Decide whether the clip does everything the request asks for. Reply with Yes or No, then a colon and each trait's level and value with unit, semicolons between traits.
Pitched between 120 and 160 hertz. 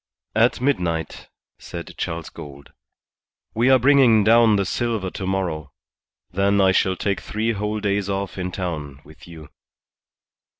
No: low, 100 Hz